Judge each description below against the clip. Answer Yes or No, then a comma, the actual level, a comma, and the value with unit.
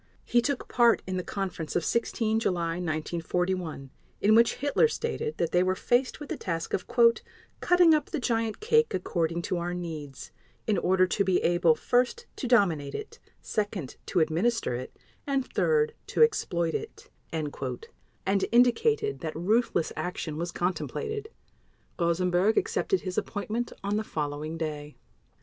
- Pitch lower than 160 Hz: No, medium, 185 Hz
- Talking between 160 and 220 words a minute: No, average, 150 wpm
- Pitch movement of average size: No, wide, 6.5 semitones